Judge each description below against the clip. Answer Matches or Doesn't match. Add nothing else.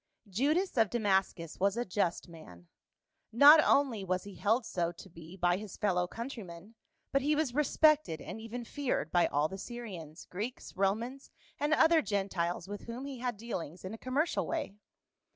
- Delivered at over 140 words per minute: Matches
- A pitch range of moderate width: Doesn't match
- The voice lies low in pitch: Doesn't match